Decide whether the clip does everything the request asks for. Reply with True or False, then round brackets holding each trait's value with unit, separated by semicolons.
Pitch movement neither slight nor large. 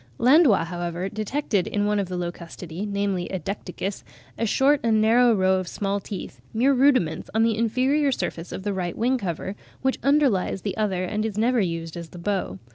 True (4.3 semitones)